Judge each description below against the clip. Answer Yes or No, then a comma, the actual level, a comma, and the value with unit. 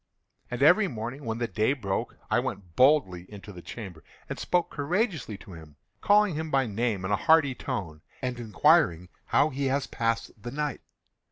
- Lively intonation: Yes, wide, 6.7 semitones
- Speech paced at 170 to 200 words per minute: Yes, average, 180 wpm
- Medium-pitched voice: No, low, 120 Hz